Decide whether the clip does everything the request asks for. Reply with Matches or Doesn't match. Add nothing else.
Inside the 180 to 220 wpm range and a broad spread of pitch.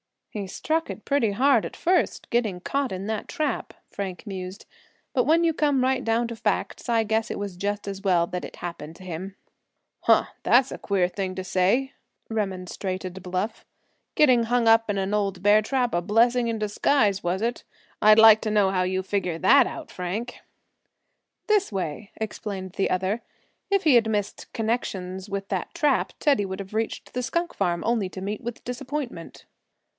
Doesn't match